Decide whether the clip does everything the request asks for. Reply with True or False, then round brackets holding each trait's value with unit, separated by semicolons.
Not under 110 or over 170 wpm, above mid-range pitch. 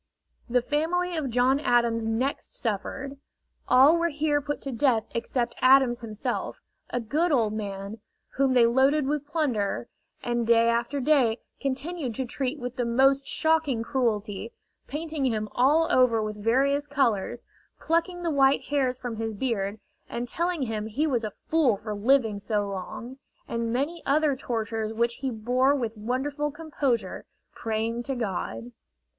True (155 wpm; 250 Hz)